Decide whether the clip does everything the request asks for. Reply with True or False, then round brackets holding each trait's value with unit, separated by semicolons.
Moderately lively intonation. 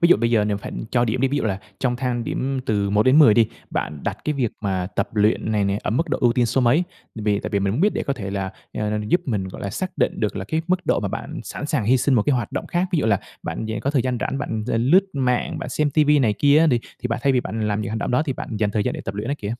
True (4.7 semitones)